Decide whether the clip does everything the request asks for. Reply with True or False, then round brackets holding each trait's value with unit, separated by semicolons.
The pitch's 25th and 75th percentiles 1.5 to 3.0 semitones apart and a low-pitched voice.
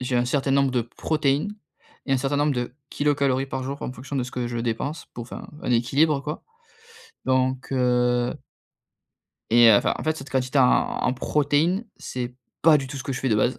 True (2.5 semitones; 130 Hz)